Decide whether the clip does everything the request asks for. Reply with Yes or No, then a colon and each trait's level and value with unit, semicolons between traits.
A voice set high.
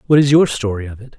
No: low, 125 Hz